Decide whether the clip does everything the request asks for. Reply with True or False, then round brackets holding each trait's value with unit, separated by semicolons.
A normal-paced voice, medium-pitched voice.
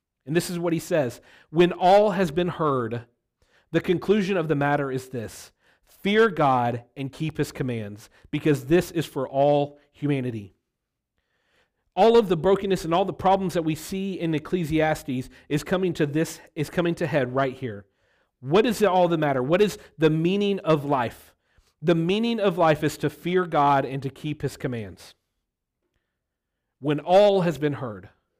True (175 wpm; 155 Hz)